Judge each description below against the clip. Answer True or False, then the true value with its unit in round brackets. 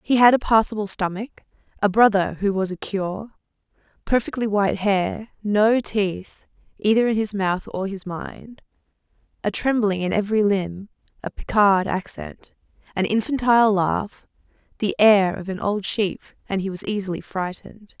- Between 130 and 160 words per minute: True (150 wpm)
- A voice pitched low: False (205 Hz)